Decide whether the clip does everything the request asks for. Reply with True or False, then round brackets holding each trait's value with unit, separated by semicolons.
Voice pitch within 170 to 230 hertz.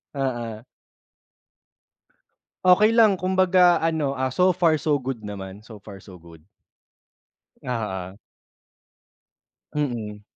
False (130 Hz)